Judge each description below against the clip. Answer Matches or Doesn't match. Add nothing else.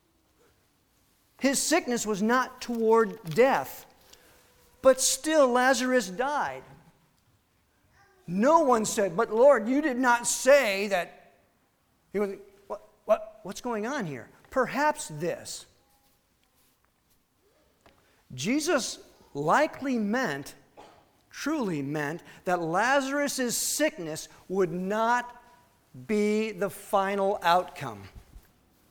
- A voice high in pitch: Matches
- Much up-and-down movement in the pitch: Matches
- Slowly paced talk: Matches